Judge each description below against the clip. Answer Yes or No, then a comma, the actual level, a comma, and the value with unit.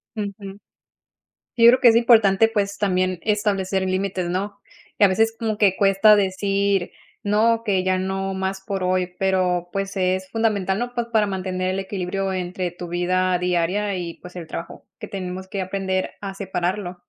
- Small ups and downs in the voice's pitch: Yes, narrow, 1.8 semitones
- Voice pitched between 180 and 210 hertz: Yes, high, 190 Hz